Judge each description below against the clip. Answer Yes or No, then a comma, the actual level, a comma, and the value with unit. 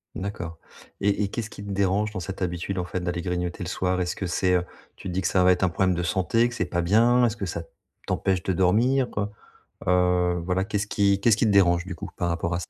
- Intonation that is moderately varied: No, narrow, 2.2 semitones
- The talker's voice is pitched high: No, very low, 95 Hz